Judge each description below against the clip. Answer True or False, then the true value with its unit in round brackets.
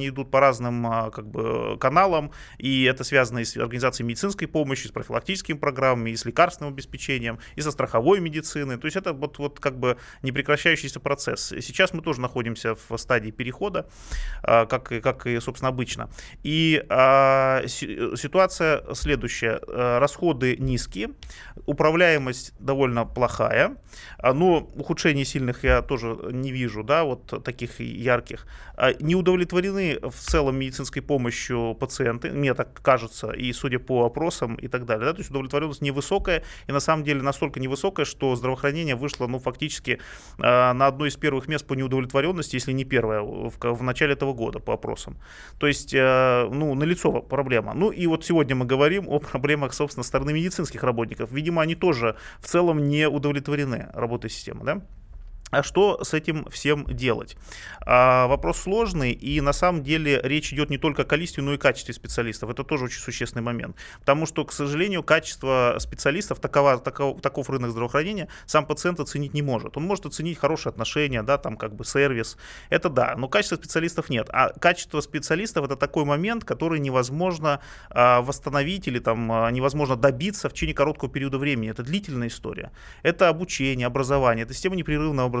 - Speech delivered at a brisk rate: True (170 wpm)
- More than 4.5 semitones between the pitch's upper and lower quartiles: False (3.6 semitones)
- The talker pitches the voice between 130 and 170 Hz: True (140 Hz)